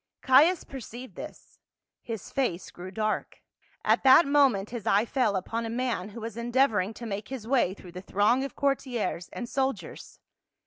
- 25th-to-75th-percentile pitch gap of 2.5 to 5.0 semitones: Yes, average, 4.4 semitones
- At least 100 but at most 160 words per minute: No, average, 170 wpm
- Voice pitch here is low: No, high, 235 Hz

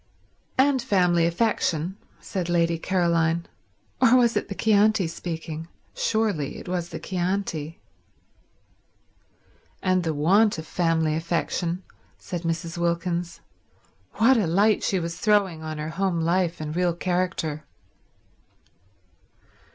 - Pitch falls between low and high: Yes, medium, 175 Hz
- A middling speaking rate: No, slow, 110 wpm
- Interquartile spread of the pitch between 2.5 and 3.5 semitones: Yes, average, 2.8 semitones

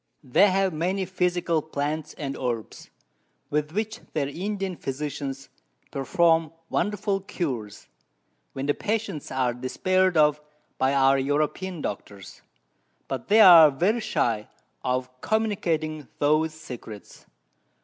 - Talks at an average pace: No, slow, 115 wpm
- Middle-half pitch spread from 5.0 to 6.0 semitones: Yes, wide, 5.6 semitones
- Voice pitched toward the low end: No, medium, 155 Hz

